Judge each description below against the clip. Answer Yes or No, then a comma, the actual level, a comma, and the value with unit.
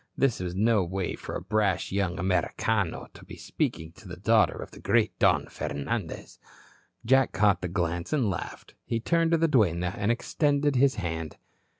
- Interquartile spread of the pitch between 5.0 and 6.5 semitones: Yes, average, 5.3 semitones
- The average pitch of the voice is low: Yes, low, 100 Hz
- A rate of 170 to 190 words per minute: Yes, average, 180 wpm